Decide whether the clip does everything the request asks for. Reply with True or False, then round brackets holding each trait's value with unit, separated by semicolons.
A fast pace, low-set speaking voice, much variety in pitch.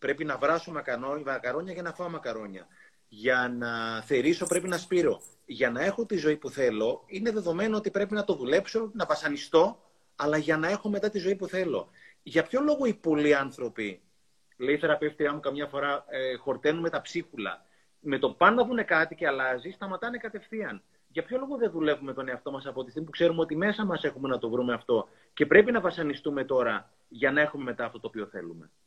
False (205 wpm; 155 Hz; 6.3 semitones)